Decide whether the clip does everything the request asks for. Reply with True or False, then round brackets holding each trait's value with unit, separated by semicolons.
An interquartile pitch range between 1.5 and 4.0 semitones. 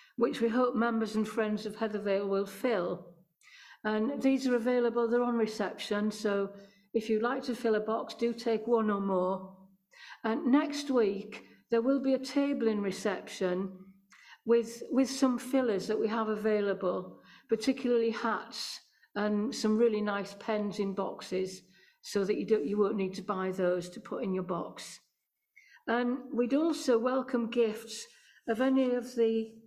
True (3.4 semitones)